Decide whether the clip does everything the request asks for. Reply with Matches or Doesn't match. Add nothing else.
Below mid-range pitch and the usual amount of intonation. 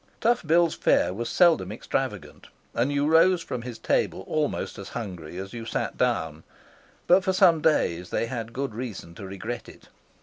Doesn't match